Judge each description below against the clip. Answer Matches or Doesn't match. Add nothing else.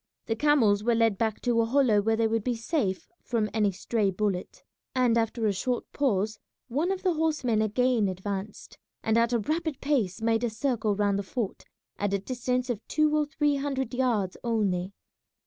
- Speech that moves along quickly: Doesn't match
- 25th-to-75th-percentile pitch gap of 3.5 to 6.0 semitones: Matches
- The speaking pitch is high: Matches